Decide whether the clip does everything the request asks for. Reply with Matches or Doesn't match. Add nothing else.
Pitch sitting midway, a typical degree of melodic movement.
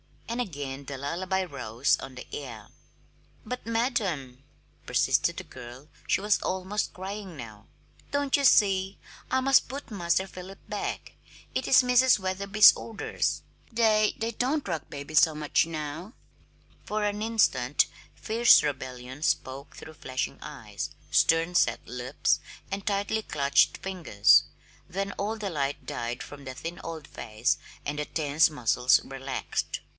Doesn't match